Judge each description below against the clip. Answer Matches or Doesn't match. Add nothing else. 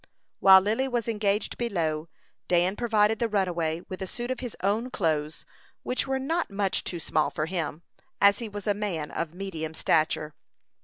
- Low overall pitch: Doesn't match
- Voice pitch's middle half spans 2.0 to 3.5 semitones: Doesn't match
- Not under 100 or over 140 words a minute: Doesn't match